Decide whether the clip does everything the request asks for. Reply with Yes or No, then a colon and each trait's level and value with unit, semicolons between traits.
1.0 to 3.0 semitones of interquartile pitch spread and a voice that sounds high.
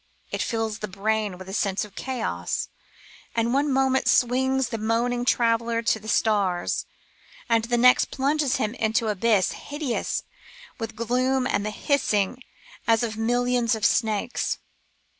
Yes: narrow, 2.6 semitones; high, 230 Hz